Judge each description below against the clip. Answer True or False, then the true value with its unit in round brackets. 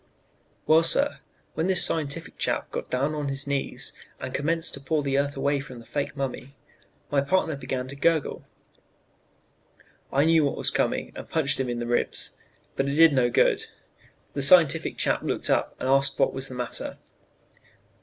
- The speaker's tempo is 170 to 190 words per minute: True (180 wpm)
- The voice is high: False (140 Hz)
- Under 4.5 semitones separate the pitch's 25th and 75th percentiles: True (2.8 semitones)